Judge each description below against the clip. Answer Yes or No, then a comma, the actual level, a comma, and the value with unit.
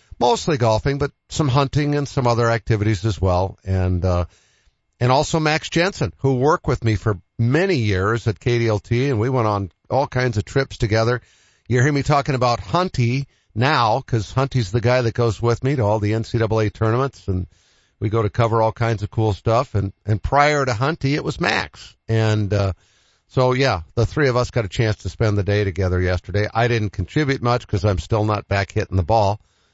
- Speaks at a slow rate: No, fast, 205 wpm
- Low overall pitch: Yes, low, 115 Hz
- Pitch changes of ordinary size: Yes, average, 4.2 semitones